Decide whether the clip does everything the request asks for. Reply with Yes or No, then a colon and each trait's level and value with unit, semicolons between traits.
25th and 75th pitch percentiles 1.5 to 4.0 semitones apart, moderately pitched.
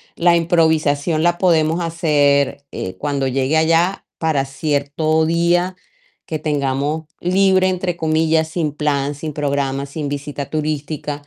Yes: average, 2.7 semitones; medium, 155 Hz